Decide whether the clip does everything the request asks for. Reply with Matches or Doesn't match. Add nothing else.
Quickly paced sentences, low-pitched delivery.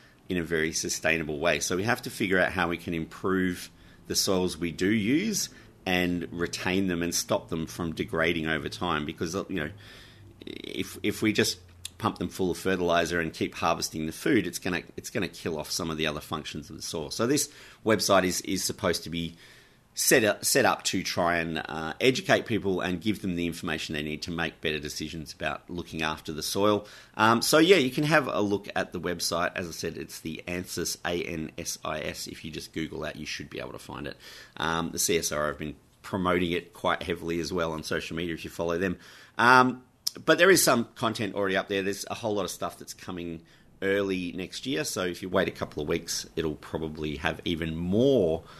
Matches